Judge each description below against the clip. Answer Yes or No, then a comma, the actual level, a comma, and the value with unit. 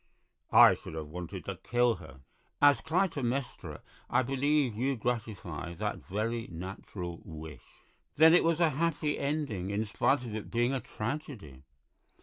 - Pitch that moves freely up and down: Yes, wide, 8.1 semitones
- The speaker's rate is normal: Yes, average, 150 wpm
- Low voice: Yes, low, 120 Hz